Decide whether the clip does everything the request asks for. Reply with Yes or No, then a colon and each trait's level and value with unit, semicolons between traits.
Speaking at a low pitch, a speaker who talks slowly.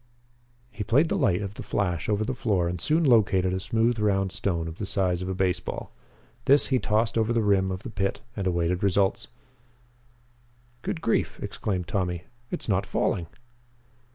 No: low, 100 Hz; average, 180 wpm